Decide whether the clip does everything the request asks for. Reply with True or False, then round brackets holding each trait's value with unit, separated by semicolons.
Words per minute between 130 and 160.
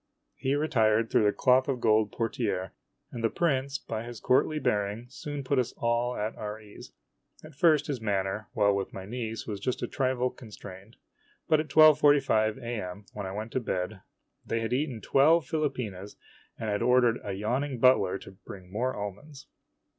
False (185 wpm)